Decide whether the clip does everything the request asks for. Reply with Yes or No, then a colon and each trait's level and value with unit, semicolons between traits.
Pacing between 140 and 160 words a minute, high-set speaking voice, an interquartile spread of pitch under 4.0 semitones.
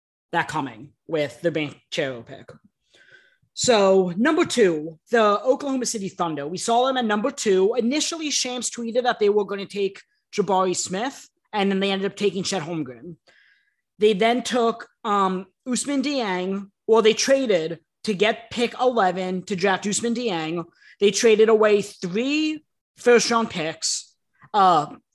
No: average, 155 wpm; high, 210 Hz; average, 4.8 semitones